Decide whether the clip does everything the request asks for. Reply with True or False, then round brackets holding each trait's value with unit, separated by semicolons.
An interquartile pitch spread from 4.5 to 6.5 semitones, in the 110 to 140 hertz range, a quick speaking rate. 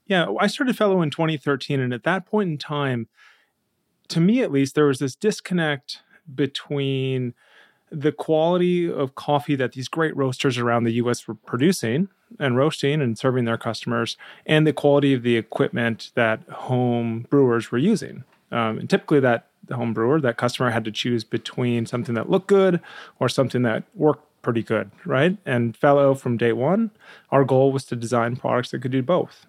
False (4.8 semitones; 135 Hz; 185 wpm)